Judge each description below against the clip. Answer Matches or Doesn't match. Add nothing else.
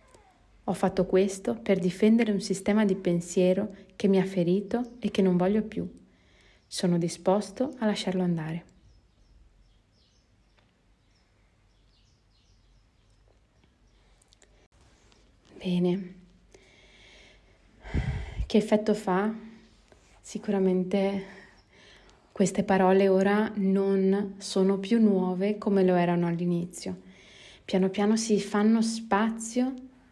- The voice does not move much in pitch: Doesn't match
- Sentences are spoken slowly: Matches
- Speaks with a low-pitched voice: Doesn't match